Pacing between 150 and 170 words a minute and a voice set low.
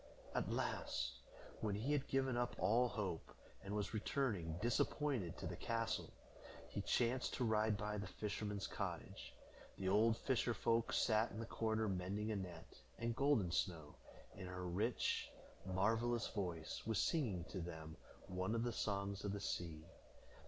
Yes: average, 160 wpm; low, 105 Hz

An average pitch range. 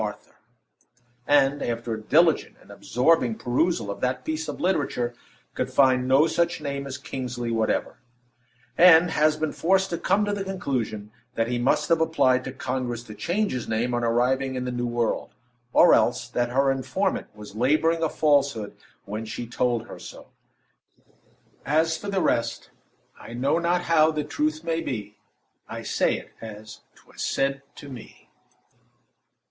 Yes: average, 5.0 semitones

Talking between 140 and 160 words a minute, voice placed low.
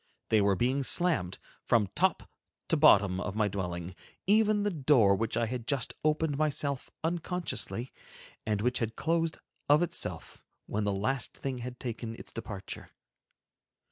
Yes: average, 150 wpm; low, 125 Hz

